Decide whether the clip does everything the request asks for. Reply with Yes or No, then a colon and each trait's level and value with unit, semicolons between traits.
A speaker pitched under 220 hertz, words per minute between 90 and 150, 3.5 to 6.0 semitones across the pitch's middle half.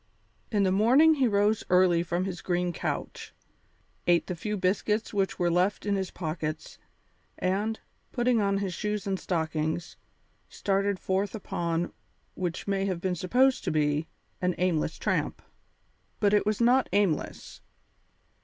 No: high, 190 Hz; average, 145 wpm; average, 3.1 semitones